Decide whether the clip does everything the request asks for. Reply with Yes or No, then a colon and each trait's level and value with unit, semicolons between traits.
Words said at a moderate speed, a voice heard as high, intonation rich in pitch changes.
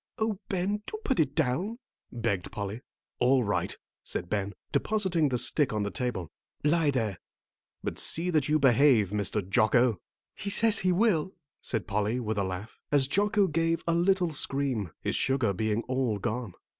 No: average, 170 wpm; low, 130 Hz; wide, 7.9 semitones